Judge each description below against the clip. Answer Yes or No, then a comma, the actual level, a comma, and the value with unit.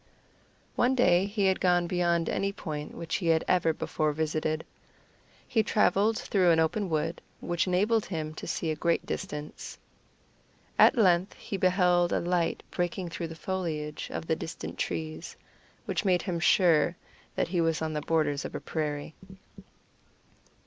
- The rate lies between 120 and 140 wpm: No, average, 160 wpm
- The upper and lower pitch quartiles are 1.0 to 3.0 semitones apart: Yes, average, 2.7 semitones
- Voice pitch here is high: No, medium, 170 Hz